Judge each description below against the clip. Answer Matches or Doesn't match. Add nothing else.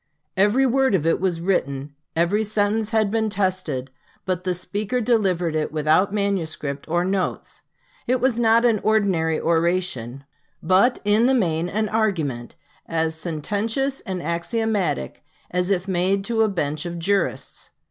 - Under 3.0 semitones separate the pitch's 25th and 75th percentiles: Doesn't match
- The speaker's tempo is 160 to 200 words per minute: Doesn't match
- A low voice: Doesn't match